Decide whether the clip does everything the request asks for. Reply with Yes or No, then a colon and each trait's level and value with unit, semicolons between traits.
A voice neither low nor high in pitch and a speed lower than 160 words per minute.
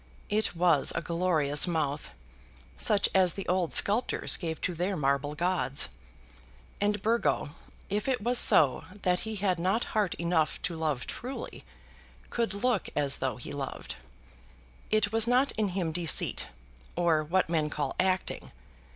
Yes: medium, 180 Hz; average, 150 wpm